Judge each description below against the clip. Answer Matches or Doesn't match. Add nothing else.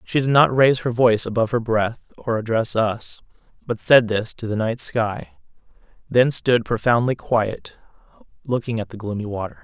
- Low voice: Matches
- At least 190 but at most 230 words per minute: Doesn't match